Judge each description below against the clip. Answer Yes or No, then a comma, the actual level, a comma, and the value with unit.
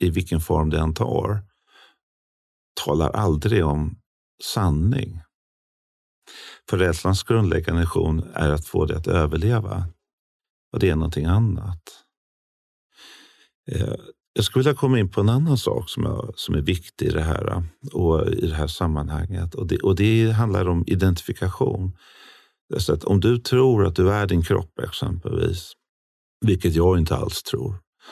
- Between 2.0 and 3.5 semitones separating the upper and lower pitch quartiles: No, average, 4.7 semitones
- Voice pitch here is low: Yes, very low, 95 Hz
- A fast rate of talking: No, average, 145 wpm